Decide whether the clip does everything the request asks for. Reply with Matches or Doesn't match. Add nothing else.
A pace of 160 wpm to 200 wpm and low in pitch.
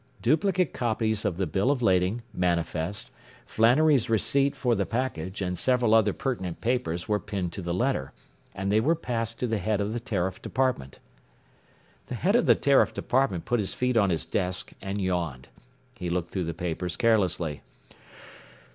Matches